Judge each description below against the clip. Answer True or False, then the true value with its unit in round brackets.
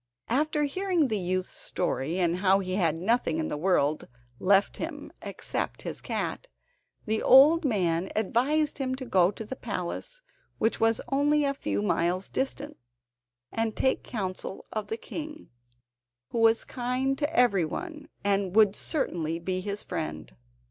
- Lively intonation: True (6.9 semitones)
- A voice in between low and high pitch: False (220 Hz)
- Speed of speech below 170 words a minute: True (150 wpm)